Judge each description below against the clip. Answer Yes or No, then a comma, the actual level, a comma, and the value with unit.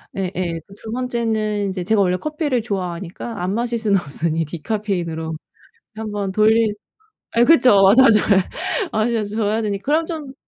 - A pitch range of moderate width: Yes, average, 3.8 semitones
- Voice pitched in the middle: No, high, 210 Hz